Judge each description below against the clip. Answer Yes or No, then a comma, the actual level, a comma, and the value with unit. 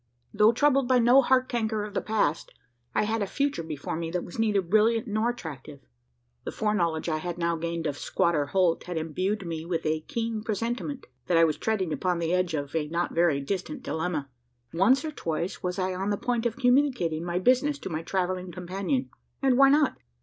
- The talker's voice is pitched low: No, medium, 185 Hz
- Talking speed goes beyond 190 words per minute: Yes, fast, 205 wpm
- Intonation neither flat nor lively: No, wide, 5.7 semitones